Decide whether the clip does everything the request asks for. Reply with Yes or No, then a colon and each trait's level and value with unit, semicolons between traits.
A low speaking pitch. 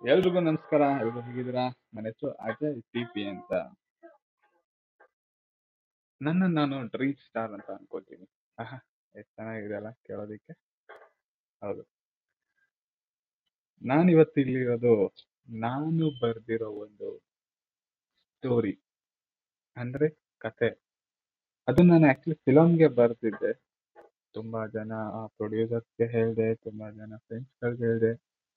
Yes: low, 120 Hz